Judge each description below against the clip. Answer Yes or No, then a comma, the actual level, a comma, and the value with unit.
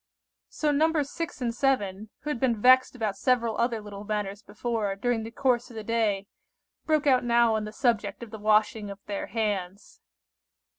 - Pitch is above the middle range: Yes, high, 225 Hz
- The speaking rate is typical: Yes, average, 185 wpm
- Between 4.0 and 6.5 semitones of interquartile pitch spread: No, average, 3.1 semitones